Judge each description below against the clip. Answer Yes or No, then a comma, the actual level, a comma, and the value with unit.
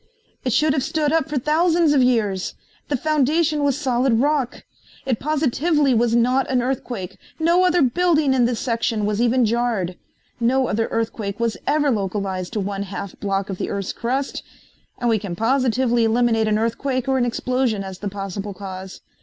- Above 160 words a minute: Yes, average, 180 wpm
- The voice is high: Yes, high, 240 Hz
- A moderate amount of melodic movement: Yes, average, 4.8 semitones